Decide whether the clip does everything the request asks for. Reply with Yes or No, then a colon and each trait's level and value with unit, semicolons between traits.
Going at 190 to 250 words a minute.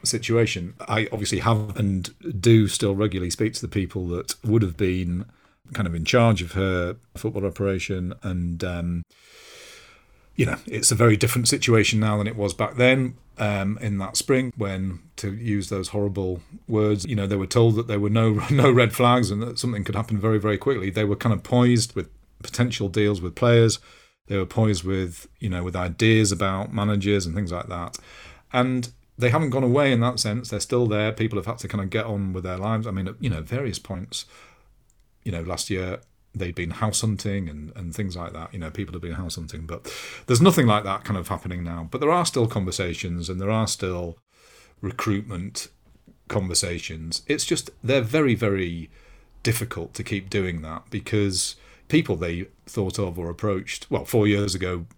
Yes: average, 200 wpm